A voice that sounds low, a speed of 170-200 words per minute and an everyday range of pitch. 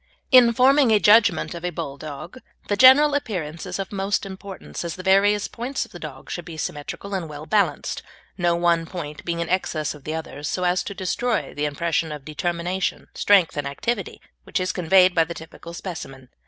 No: medium, 175 Hz; average, 195 wpm; average, 4.0 semitones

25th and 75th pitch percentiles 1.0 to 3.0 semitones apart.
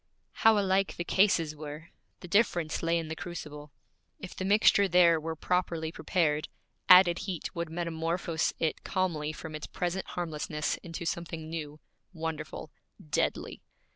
Yes: narrow, 2.4 semitones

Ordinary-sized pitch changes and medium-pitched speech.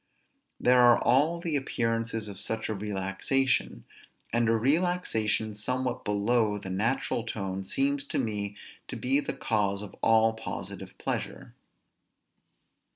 No: average, 3.8 semitones; low, 115 Hz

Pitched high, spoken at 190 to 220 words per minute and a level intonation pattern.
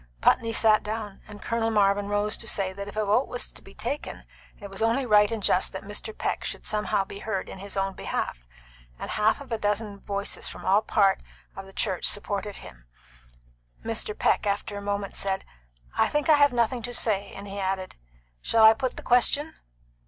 Yes: high, 205 Hz; fast, 205 wpm; narrow, 2.3 semitones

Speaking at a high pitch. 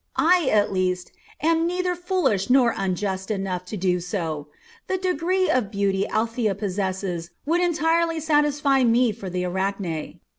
Yes: high, 215 Hz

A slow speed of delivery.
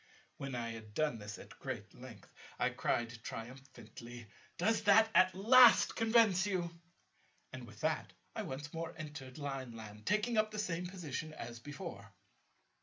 No: average, 150 wpm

